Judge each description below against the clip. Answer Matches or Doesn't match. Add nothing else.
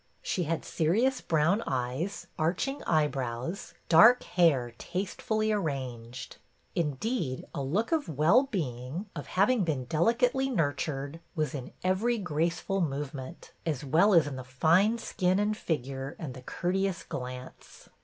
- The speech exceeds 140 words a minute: Doesn't match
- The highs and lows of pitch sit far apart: Matches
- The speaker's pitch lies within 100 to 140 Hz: Doesn't match